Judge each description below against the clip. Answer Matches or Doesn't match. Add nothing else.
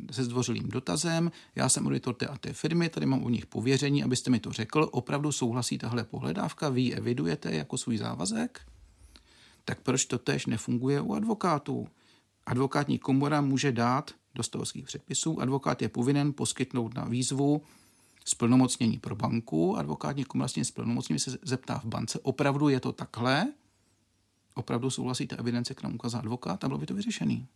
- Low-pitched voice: Matches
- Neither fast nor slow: Matches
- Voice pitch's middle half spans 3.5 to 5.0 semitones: Doesn't match